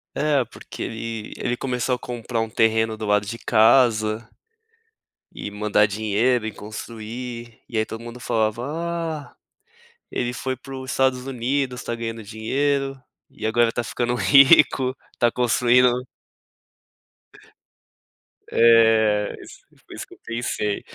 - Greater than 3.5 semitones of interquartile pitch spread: No, narrow, 2.4 semitones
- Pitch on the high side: No, low, 115 Hz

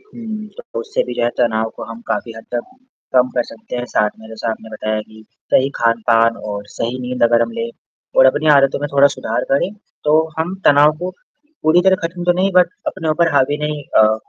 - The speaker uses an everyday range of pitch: No, wide, 7.2 semitones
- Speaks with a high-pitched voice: No, medium, 140 Hz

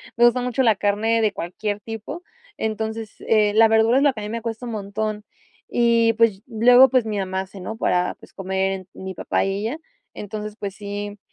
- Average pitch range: No, narrow, 2.2 semitones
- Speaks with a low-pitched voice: No, high, 215 Hz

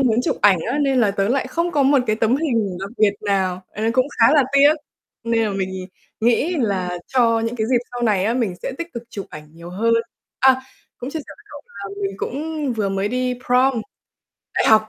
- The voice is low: No, high, 230 Hz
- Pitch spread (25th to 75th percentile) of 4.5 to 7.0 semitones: Yes, average, 4.8 semitones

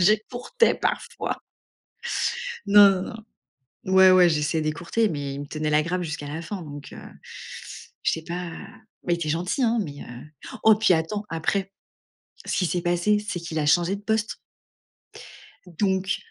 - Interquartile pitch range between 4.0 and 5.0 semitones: Yes, average, 4.6 semitones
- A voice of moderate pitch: Yes, medium, 175 Hz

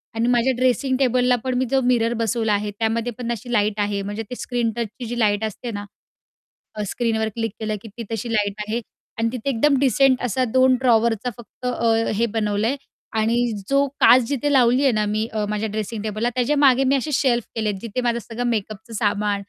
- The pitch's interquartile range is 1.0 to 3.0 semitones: Yes, average, 2.7 semitones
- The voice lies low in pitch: No, high, 230 Hz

